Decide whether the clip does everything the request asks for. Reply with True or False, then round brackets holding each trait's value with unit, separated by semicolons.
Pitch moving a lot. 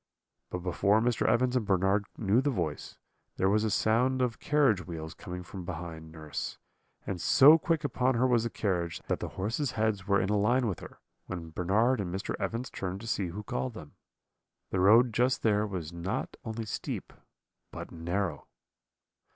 False (4.8 semitones)